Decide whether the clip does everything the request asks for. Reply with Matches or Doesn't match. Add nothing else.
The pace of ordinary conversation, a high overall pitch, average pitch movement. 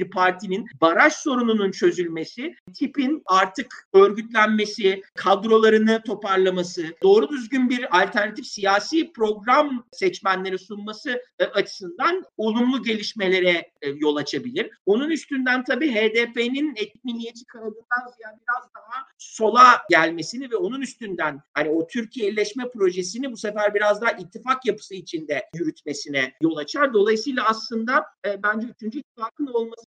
Matches